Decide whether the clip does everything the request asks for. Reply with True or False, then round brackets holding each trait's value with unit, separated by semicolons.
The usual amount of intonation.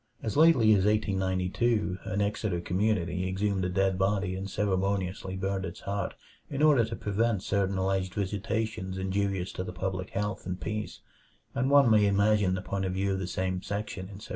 False (2.0 semitones)